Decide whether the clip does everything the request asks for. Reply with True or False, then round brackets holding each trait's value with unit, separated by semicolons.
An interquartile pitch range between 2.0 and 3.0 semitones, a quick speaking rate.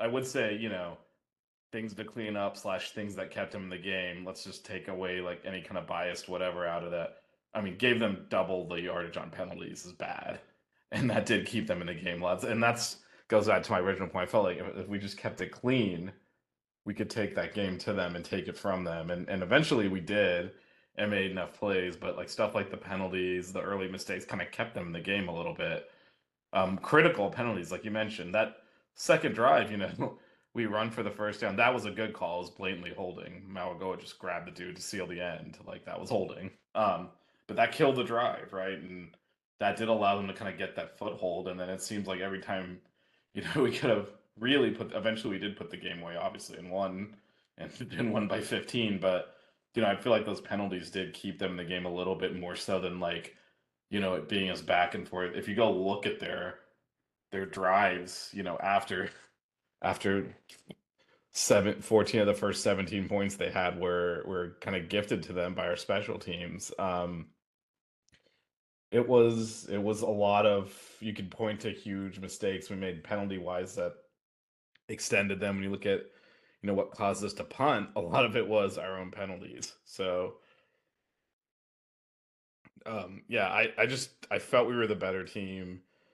True (2.4 semitones; 215 wpm)